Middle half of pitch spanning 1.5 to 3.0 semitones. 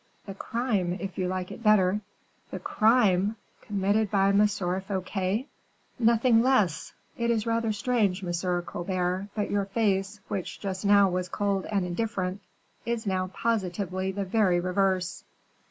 Yes: narrow, 2.6 semitones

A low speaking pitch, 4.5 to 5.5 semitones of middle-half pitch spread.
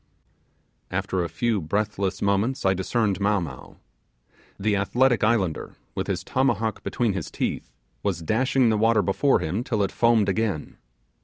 No: low, 105 Hz; average, 3.3 semitones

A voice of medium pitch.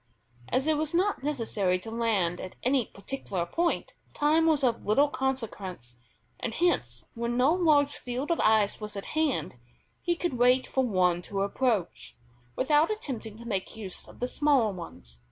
No: high, 245 Hz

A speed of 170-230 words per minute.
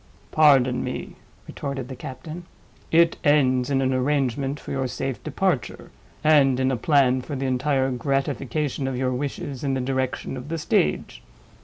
No: average, 160 wpm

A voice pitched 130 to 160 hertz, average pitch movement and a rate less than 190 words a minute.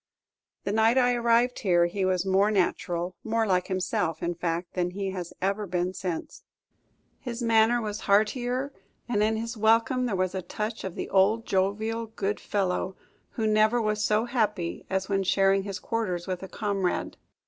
No: high, 205 Hz; average, 3.3 semitones; average, 175 wpm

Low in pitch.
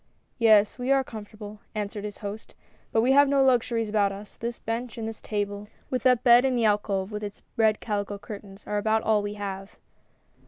No: high, 215 Hz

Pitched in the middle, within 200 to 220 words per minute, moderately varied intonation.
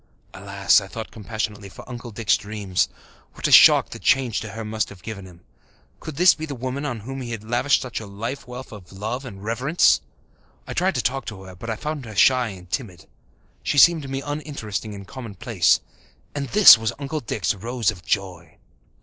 No: low, 115 Hz; fast, 205 wpm; average, 5.0 semitones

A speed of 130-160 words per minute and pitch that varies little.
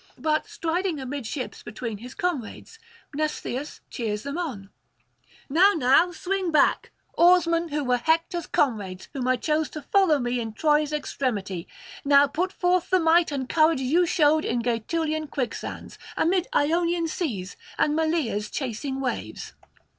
No: average, 140 wpm; average, 5.1 semitones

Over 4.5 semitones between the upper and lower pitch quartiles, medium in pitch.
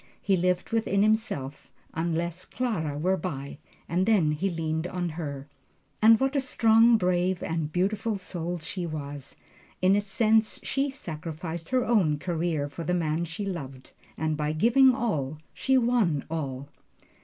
Yes: wide, 5.6 semitones; medium, 175 Hz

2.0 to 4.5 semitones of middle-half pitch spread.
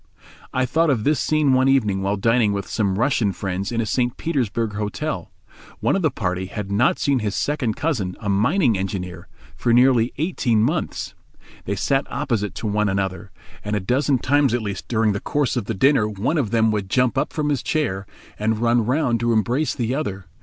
No: average, 4.9 semitones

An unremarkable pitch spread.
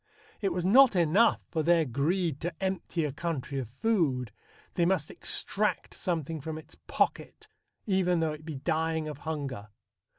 Yes: average, 3.5 semitones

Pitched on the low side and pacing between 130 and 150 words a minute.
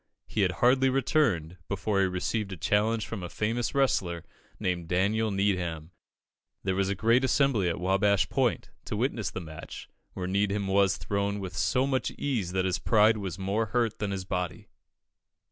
No: low, 100 Hz; average, 175 wpm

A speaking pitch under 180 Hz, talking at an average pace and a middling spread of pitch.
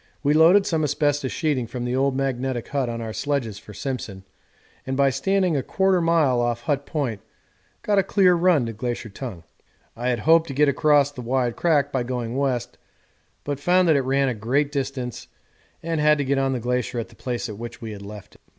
No: low, 135 Hz; fast, 215 wpm; average, 3.6 semitones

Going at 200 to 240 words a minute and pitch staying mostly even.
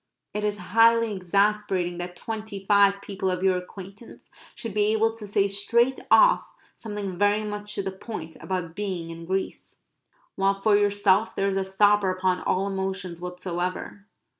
No: average, 165 wpm; narrow, 2.0 semitones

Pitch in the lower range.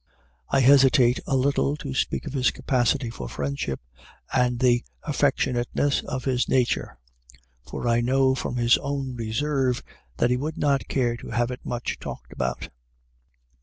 Yes: low, 125 Hz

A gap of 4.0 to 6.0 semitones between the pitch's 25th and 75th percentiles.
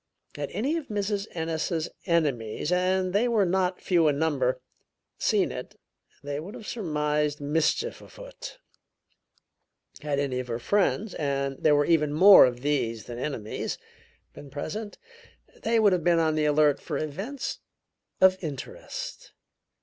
Yes: wide, 5.6 semitones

